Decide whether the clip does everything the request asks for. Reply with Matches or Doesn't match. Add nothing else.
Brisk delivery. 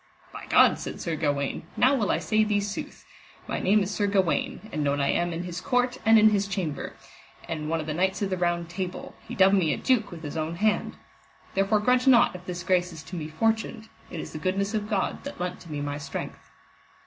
Matches